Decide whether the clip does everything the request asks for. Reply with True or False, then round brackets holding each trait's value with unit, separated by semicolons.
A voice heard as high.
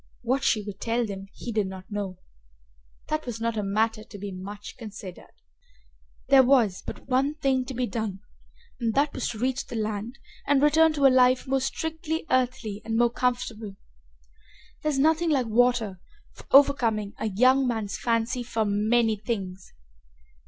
True (235 Hz)